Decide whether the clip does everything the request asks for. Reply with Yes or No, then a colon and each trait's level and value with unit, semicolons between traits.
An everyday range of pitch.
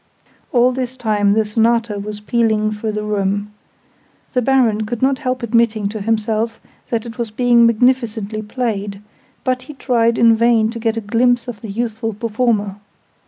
No: narrow, 2.3 semitones